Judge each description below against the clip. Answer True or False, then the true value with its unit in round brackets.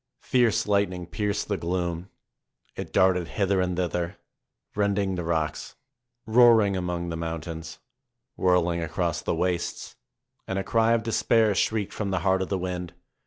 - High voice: False (95 Hz)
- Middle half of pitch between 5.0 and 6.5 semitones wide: False (2.7 semitones)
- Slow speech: False (155 wpm)